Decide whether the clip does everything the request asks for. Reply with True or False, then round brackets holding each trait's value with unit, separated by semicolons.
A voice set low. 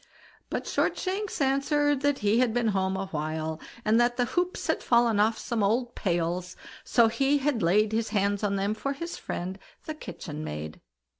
False (220 Hz)